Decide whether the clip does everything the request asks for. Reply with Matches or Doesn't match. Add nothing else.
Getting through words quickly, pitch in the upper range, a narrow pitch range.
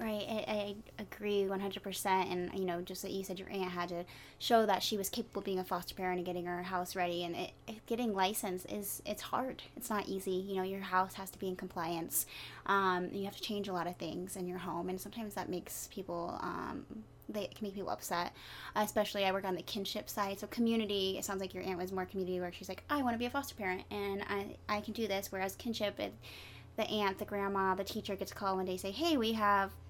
Matches